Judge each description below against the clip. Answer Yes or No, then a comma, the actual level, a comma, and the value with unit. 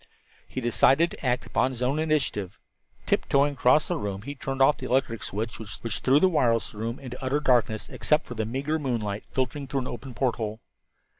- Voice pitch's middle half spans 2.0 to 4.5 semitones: Yes, average, 3.4 semitones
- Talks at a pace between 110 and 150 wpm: No, average, 195 wpm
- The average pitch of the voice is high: No, low, 130 Hz